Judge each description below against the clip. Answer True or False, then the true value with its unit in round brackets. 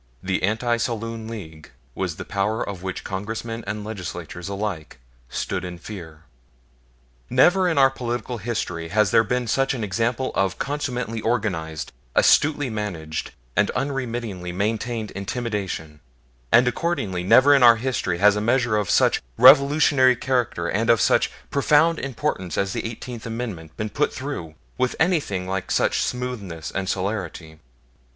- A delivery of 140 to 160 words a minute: True (145 wpm)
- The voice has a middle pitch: False (110 Hz)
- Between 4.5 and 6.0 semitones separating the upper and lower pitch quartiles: True (4.9 semitones)